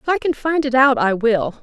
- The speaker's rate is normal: No, fast, 295 wpm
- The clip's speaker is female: Yes, female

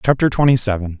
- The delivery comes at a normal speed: Yes, average, 180 wpm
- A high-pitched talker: No, low, 115 Hz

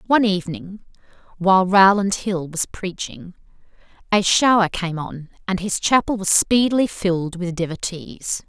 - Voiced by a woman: Yes, female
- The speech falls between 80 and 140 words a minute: Yes, slow, 135 wpm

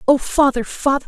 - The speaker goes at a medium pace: Yes, average, 170 wpm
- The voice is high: Yes, very high, 270 Hz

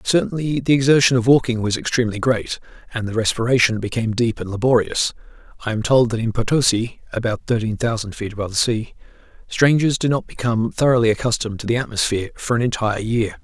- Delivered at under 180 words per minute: No, average, 185 wpm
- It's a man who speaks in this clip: Yes, male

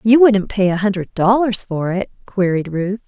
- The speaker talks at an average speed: Yes, average, 195 wpm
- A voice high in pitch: Yes, high, 200 Hz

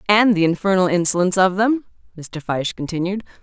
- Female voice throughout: Yes, female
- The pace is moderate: Yes, average, 160 wpm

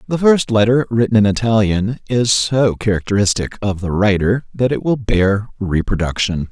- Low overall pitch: Yes, low, 110 Hz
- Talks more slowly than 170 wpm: Yes, average, 155 wpm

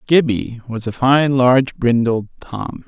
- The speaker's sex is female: No, male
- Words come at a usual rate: Yes, average, 145 wpm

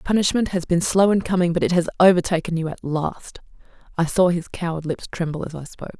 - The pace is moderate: No, fast, 220 wpm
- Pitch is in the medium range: Yes, medium, 175 Hz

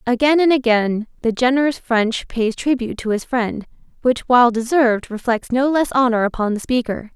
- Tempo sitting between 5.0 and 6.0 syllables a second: Yes, 5.3 syllables/s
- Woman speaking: Yes, female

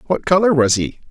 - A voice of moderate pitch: Yes, medium, 155 Hz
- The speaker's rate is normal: No, fast, 215 wpm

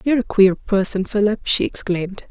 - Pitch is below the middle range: No, high, 205 Hz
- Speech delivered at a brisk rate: No, average, 180 wpm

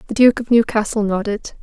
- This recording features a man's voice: No, female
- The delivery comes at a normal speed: Yes, average, 185 wpm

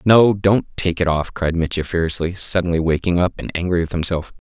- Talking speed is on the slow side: No, average, 200 wpm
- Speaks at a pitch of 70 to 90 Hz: Yes, very low, 85 Hz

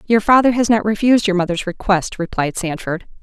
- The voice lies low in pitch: No, high, 200 Hz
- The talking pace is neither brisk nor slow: Yes, average, 185 wpm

